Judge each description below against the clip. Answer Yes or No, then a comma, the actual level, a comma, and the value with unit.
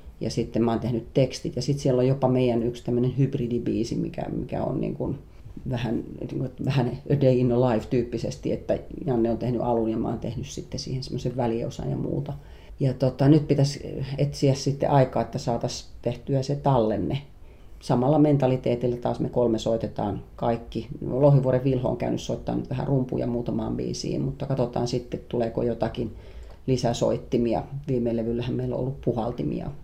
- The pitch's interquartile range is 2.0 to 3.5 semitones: Yes, average, 2.7 semitones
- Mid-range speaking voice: No, low, 125 Hz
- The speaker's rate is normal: No, fast, 170 wpm